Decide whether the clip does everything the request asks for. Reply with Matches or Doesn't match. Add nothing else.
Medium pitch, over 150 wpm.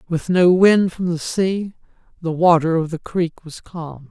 Matches